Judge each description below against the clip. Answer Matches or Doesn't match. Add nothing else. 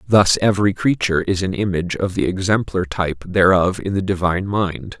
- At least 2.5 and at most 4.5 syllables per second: Doesn't match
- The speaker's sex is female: Doesn't match